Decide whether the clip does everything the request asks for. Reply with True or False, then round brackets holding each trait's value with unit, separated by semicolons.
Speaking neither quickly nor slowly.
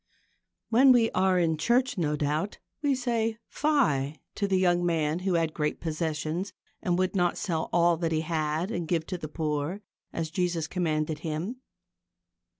True (165 wpm)